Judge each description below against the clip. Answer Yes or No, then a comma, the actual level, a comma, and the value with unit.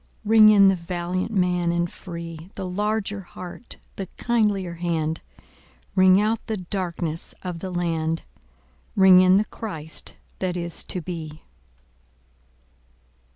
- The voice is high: No, medium, 180 Hz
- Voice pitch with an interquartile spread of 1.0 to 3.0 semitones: Yes, narrow, 2.6 semitones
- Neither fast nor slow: No, slow, 125 wpm